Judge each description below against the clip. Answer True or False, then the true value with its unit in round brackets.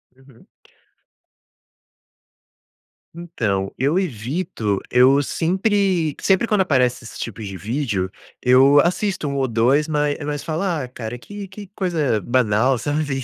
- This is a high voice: False (140 Hz)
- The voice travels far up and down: True (6.0 semitones)